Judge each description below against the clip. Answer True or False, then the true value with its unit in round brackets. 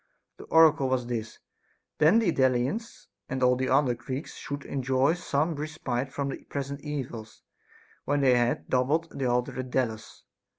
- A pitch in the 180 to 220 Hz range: False (135 Hz)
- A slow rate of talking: False (165 wpm)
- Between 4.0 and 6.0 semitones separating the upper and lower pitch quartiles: False (2.8 semitones)